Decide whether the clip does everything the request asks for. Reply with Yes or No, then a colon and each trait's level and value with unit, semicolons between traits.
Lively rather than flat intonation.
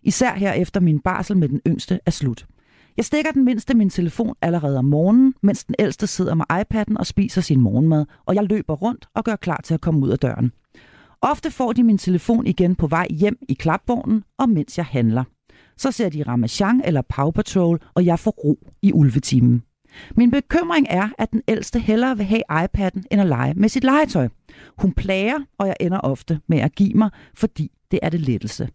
Yes: wide, 6.1 semitones